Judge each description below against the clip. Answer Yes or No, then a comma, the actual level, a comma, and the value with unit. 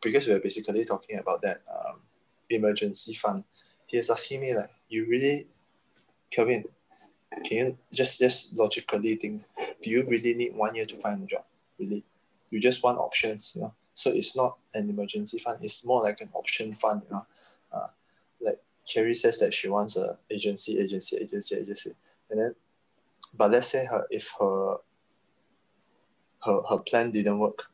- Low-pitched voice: Yes, low, 120 Hz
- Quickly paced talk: No, average, 170 wpm